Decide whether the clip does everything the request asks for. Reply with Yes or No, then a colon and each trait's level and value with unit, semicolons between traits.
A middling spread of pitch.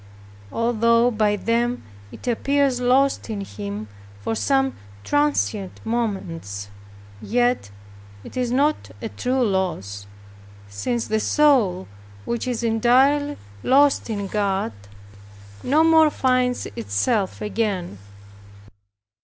Yes: average, 4.8 semitones